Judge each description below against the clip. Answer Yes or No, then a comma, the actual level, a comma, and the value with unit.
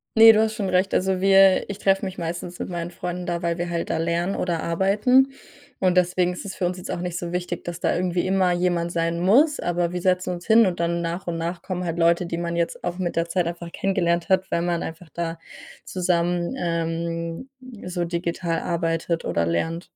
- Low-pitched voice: No, medium, 175 Hz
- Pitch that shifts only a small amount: Yes, narrow, 1.6 semitones